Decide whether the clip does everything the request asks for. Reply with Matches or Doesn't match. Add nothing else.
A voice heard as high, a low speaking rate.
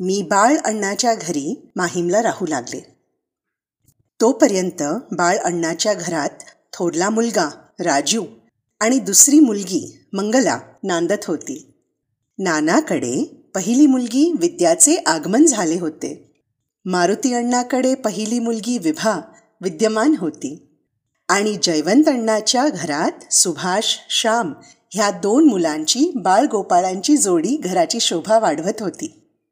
Doesn't match